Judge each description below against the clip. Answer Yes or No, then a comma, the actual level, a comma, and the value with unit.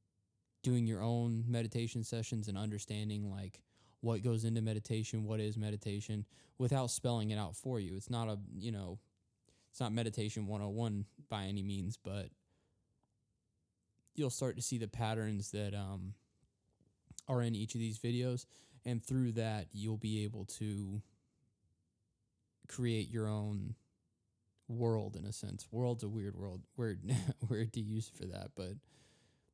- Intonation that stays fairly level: Yes, narrow, 2.3 semitones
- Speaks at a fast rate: No, average, 150 wpm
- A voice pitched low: Yes, low, 110 Hz